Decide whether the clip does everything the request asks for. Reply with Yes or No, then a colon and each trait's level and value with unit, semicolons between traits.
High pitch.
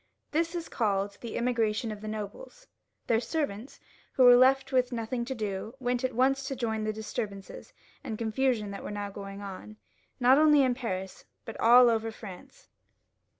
Yes: high, 230 Hz